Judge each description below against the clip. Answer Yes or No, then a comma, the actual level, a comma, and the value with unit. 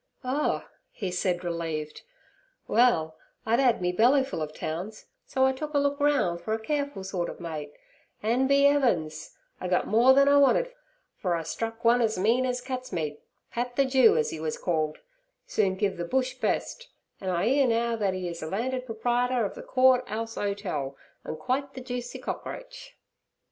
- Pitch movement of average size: No, wide, 6.6 semitones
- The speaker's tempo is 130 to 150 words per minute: No, average, 185 wpm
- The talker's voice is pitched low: No, high, 225 Hz